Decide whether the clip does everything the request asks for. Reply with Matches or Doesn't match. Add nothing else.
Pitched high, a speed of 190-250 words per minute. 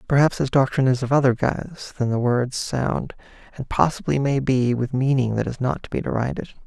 Doesn't match